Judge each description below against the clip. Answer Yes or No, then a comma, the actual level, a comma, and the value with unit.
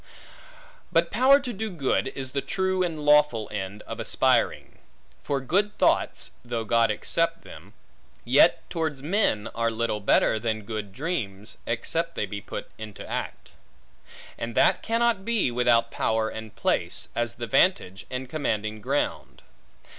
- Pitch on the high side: No, low, 125 Hz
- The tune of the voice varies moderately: No, wide, 7.3 semitones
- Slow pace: No, average, 145 wpm